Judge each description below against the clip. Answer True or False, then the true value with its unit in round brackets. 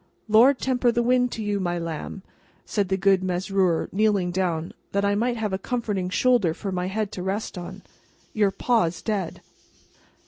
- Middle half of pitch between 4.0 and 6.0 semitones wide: False (3.3 semitones)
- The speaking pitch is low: False (195 Hz)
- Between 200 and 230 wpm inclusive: False (175 wpm)